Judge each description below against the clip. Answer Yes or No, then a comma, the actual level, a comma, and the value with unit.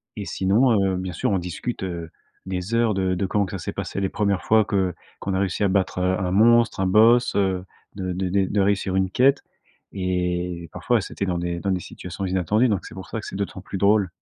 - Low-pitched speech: Yes, very low, 95 Hz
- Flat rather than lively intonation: Yes, narrow, 1.9 semitones